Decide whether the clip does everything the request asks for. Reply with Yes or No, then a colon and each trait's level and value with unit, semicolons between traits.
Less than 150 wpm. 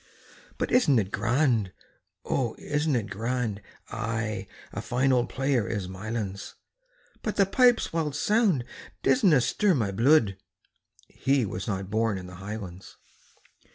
Yes: slow, 135 wpm